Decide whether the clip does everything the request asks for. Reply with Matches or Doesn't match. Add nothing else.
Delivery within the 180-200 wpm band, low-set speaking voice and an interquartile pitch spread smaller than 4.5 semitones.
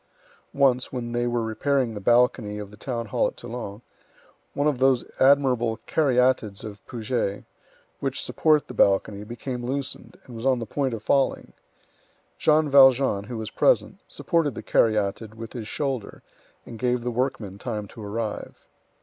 Doesn't match